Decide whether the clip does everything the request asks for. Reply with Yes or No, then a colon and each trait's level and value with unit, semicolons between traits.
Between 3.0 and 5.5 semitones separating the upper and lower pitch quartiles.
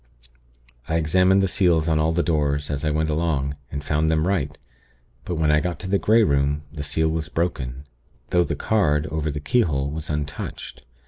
No: narrow, 2.6 semitones